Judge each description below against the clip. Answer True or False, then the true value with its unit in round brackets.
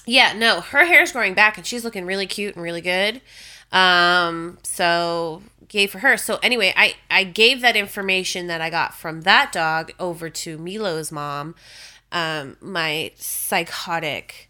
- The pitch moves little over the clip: False (3.7 semitones)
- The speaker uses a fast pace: False (160 wpm)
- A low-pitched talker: False (180 Hz)